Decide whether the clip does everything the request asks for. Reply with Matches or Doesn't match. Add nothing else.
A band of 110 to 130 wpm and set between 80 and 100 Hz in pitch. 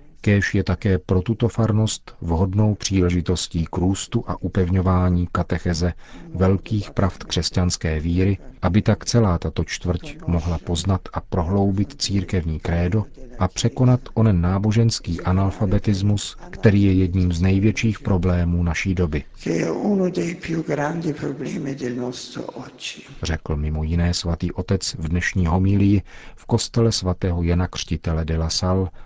Matches